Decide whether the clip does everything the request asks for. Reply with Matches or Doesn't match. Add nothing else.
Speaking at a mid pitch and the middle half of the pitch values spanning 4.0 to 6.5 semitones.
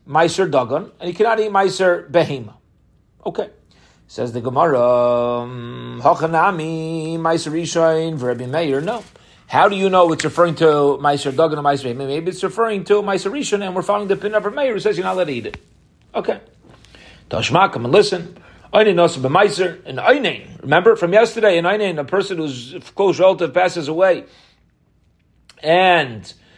Matches